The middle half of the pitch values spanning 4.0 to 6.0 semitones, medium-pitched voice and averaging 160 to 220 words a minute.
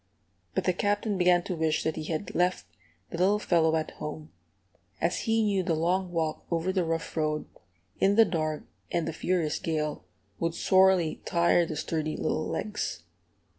No: average, 2.9 semitones; medium, 170 Hz; average, 170 wpm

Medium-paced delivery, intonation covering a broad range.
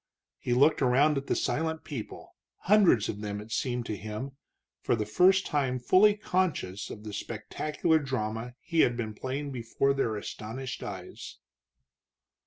Yes: average, 155 wpm; wide, 5.8 semitones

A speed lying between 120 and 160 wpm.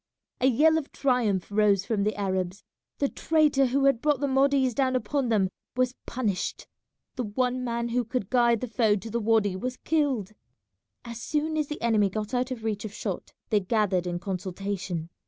No: average, 190 wpm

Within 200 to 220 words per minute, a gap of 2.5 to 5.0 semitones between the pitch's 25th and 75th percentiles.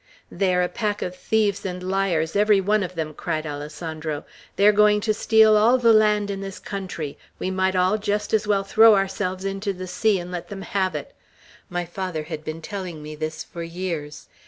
Yes: fast, 205 wpm; average, 3.5 semitones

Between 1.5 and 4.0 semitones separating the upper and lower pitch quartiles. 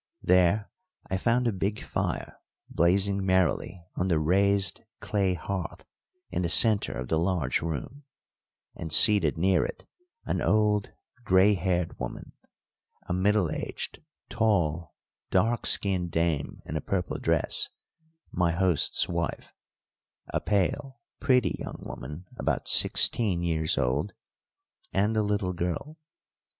Yes: average, 3.4 semitones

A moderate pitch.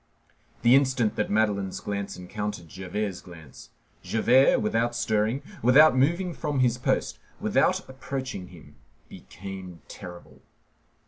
No: low, 110 Hz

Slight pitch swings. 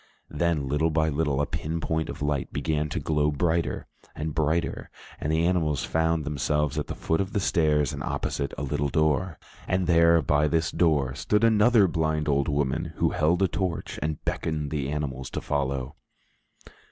Yes: narrow, 2.3 semitones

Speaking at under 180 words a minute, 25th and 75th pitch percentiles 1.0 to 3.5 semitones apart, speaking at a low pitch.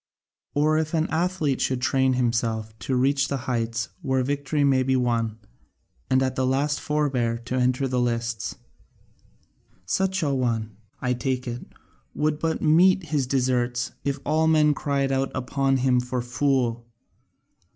Yes: average, 160 wpm; average, 2.9 semitones; low, 130 Hz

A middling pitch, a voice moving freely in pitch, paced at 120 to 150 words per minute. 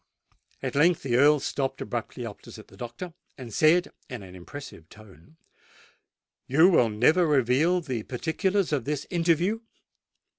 Yes: medium, 145 Hz; wide, 5.9 semitones; average, 140 wpm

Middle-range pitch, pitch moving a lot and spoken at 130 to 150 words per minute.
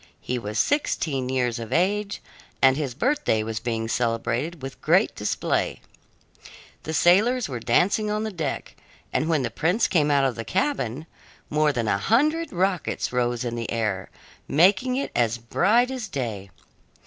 No: medium, 145 Hz; wide, 9.0 semitones; average, 160 wpm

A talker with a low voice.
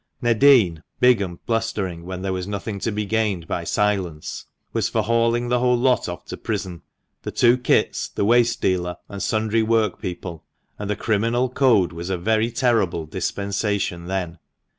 Yes: low, 105 Hz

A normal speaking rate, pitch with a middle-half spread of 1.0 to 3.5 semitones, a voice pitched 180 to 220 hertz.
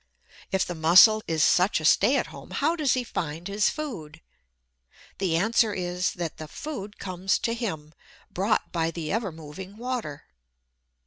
No: average, 165 wpm; wide, 5.4 semitones; medium, 185 Hz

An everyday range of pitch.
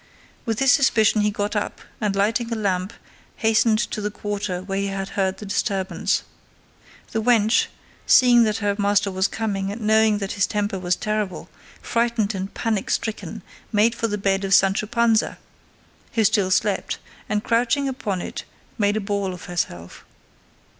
No: narrow, 2.2 semitones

